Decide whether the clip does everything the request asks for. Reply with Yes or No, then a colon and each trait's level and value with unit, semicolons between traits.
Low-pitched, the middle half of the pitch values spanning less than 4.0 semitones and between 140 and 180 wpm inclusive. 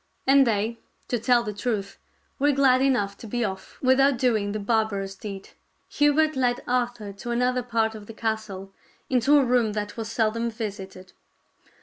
No: high, 230 Hz; average, 3.4 semitones; average, 165 wpm